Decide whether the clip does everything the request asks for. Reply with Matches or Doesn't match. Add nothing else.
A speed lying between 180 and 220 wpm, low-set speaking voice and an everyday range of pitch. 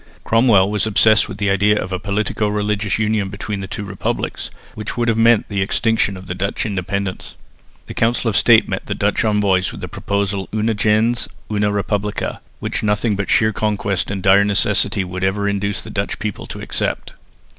Doesn't match